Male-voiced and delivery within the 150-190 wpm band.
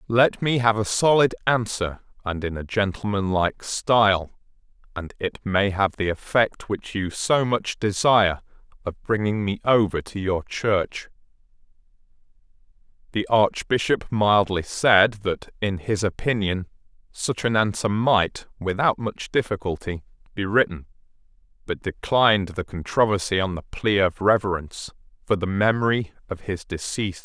No: male; slow, 135 wpm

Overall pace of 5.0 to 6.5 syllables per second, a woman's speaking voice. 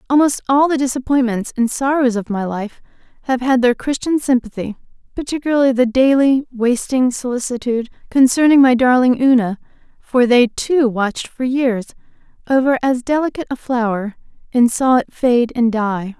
Yes: 5.1 syllables/s; female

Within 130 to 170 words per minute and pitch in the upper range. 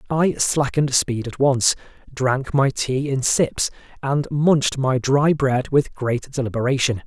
No: average, 155 wpm; low, 135 Hz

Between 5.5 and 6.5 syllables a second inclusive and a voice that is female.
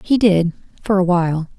No: 5.3 syllables/s; female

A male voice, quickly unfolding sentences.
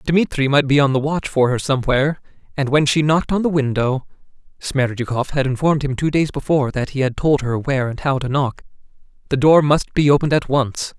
Yes: male; fast, 220 wpm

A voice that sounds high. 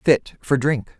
No: low, 135 Hz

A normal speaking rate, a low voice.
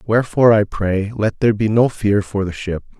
No: fast, 220 wpm; low, 105 Hz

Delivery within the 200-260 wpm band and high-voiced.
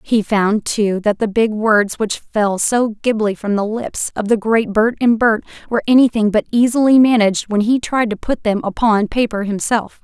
Yes: fast, 205 wpm; high, 220 Hz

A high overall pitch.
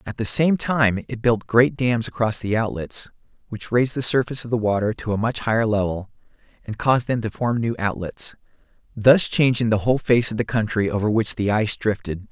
No: low, 115 Hz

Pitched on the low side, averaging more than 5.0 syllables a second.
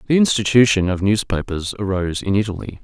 Yes: low, 105 Hz; 6.1 syllables/s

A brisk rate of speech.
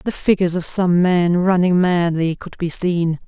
No: average, 185 wpm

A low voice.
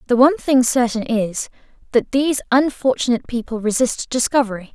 No: high, 245 Hz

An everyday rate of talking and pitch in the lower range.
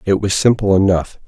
Yes: average, 190 wpm; low, 100 Hz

